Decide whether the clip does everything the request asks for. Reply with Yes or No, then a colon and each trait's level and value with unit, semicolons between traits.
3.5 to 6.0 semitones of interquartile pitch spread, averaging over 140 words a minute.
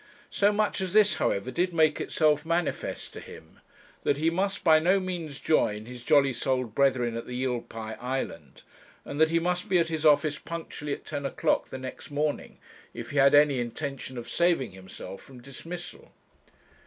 Yes: average, 4.8 semitones; average, 185 wpm